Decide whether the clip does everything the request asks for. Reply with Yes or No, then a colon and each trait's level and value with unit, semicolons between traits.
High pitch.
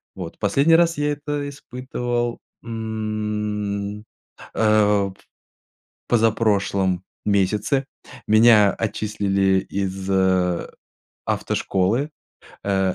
No: low, 105 Hz